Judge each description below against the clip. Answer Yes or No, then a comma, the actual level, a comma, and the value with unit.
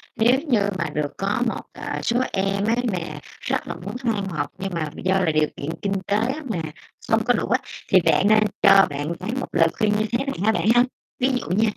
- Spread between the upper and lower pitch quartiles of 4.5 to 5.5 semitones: Yes, average, 4.9 semitones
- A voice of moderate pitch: No, high, 195 Hz